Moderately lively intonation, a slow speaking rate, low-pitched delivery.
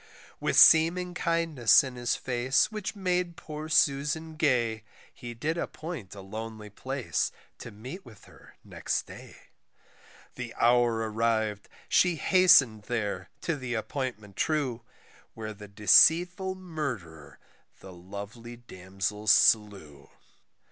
No: wide, 6.9 semitones; slow, 120 wpm; low, 120 Hz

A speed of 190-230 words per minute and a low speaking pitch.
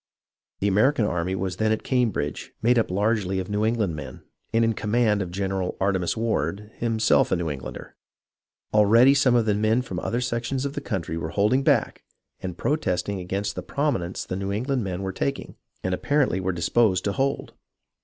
Yes: average, 195 wpm; low, 105 Hz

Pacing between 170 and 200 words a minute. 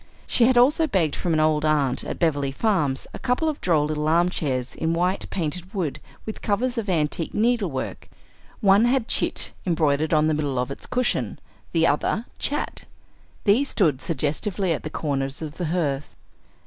Yes: average, 175 wpm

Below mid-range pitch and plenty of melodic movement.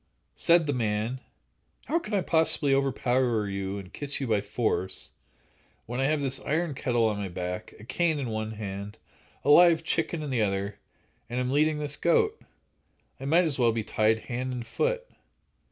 Yes: low, 125 Hz; wide, 6.0 semitones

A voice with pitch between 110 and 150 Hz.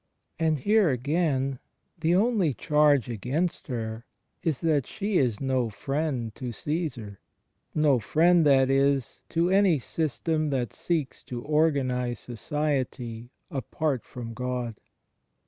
Yes: medium, 140 Hz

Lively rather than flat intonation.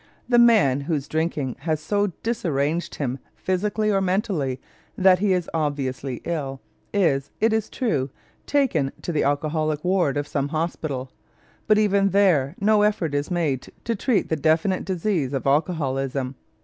Yes: wide, 5.9 semitones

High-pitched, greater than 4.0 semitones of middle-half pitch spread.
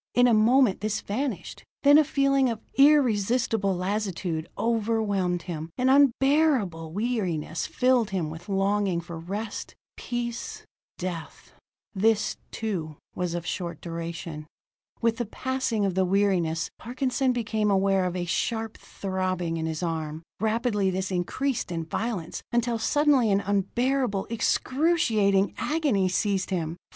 Yes: high, 205 Hz; average, 5.2 semitones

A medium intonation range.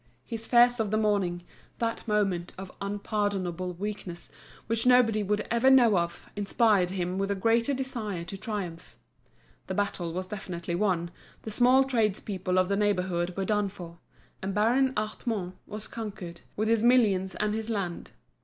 Yes: average, 3.4 semitones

